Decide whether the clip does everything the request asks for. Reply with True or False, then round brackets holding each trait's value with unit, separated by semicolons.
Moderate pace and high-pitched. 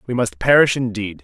False (195 wpm; 115 Hz)